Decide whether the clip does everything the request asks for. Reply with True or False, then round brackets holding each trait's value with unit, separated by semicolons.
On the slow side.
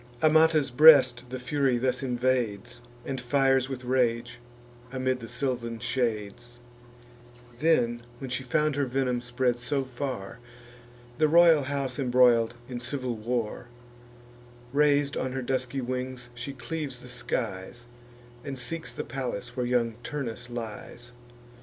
True (130 wpm)